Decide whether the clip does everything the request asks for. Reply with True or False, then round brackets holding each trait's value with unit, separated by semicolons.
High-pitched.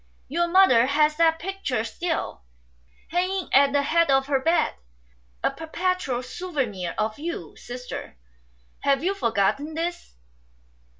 True (300 Hz)